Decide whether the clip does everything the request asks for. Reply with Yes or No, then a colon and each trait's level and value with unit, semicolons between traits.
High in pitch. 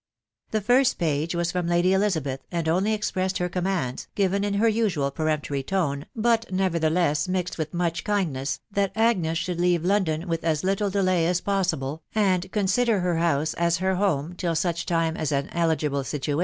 No: medium, 175 Hz